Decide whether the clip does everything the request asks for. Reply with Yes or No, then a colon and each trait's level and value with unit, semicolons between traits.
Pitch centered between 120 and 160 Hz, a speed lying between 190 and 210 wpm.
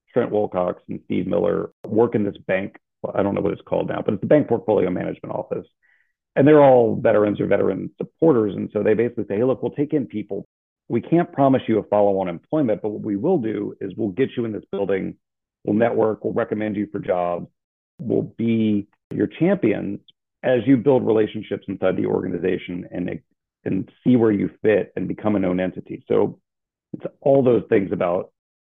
No: low, 105 Hz; average, 200 wpm